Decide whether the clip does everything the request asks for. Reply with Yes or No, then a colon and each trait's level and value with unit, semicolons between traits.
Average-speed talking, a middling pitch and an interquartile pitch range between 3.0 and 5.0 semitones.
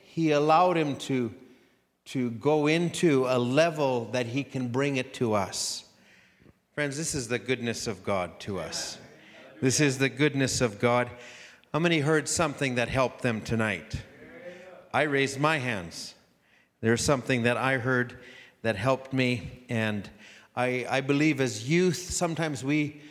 No: average, 155 wpm; low, 130 Hz; average, 3.5 semitones